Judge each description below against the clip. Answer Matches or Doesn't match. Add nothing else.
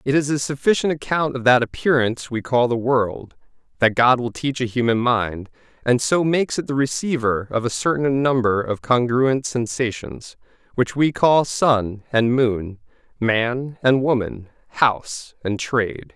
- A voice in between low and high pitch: Doesn't match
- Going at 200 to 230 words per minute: Doesn't match